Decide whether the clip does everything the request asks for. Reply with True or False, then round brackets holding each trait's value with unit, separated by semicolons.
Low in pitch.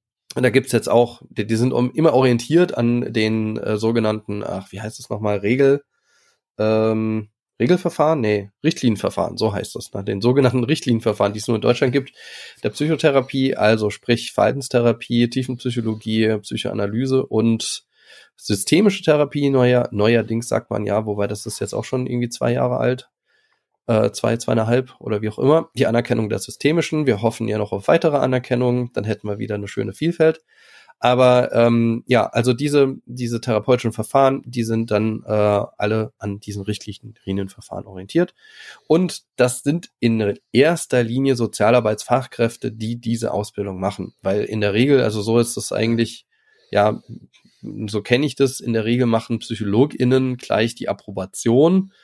True (120 Hz)